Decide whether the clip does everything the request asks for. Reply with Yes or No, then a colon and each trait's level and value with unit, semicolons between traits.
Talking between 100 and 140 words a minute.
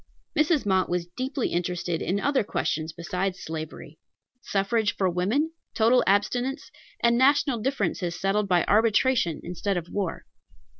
Yes: slow, 135 wpm